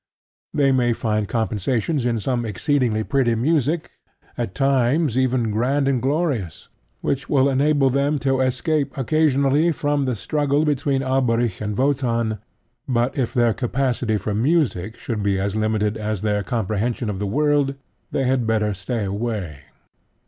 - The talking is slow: No, average, 150 wpm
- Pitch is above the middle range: No, low, 125 Hz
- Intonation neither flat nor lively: Yes, average, 4.2 semitones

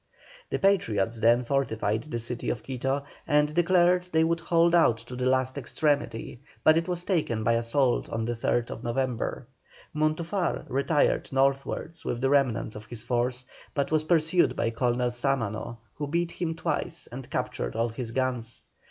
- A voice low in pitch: Yes, low, 130 Hz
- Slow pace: No, average, 165 wpm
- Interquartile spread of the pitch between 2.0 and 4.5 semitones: No, average, 5.0 semitones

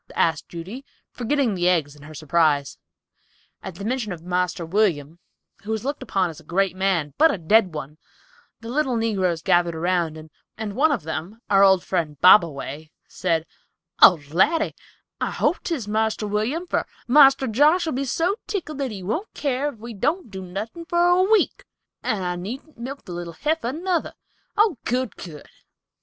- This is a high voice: Yes, high, 205 Hz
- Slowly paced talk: No, average, 175 wpm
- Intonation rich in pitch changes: Yes, wide, 7.9 semitones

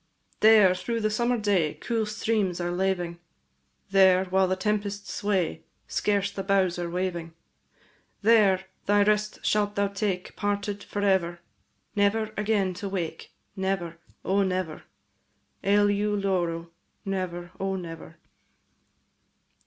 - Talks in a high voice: Yes, high, 195 Hz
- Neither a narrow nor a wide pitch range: No, narrow, 2.2 semitones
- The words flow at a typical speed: No, slow, 120 wpm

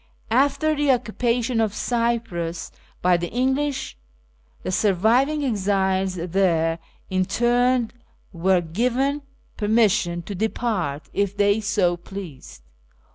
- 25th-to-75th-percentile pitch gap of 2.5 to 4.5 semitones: No, average, 5.2 semitones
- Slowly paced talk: Yes, slow, 105 wpm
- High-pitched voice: Yes, high, 205 Hz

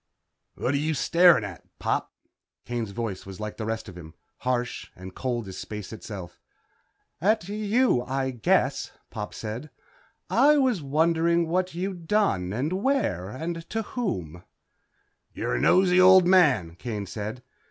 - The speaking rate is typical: Yes, average, 150 wpm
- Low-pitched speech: Yes, low, 130 Hz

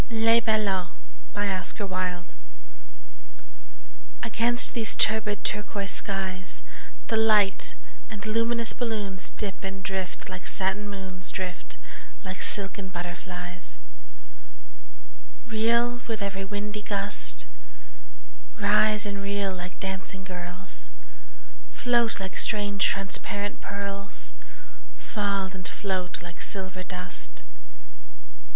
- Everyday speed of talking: No, slow, 90 wpm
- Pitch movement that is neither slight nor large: No, narrow, 2.1 semitones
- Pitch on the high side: Yes, high, 200 Hz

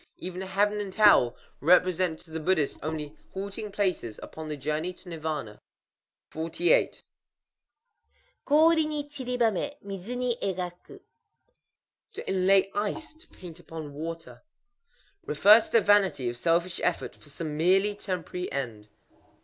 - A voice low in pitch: No, medium, 185 Hz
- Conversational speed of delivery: No, slow, 125 wpm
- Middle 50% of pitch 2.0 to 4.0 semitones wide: No, average, 4.6 semitones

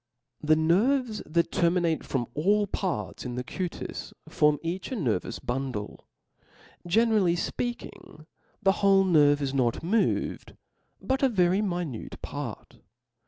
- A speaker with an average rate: No, slow, 125 wpm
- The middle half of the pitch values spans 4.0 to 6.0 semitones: Yes, wide, 5.6 semitones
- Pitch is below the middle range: No, medium, 175 Hz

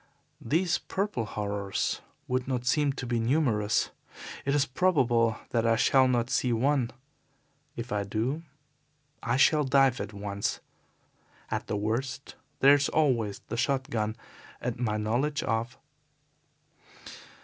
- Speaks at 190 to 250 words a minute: No, slow, 135 wpm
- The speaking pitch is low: Yes, low, 120 Hz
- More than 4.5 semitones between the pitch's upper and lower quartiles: No, average, 3.8 semitones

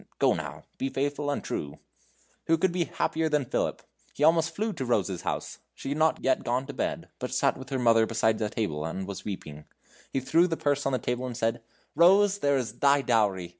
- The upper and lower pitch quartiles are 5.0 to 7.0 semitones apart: Yes, wide, 5.6 semitones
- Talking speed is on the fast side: Yes, fast, 220 wpm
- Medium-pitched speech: No, low, 130 Hz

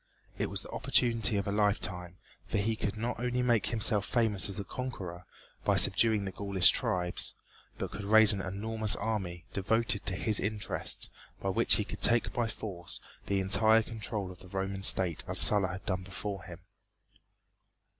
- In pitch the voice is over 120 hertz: No, low, 100 Hz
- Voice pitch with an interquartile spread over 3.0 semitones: No, average, 2.7 semitones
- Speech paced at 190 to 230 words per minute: No, average, 175 wpm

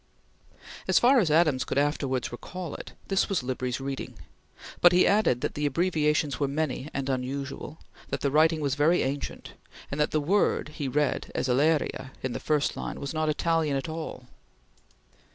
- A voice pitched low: No, medium, 150 Hz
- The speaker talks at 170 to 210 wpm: Yes, average, 175 wpm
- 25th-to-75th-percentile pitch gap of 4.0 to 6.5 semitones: No, average, 3.0 semitones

